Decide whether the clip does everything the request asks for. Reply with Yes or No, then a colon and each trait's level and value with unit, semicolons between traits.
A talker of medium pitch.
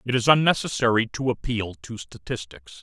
No: low, 115 Hz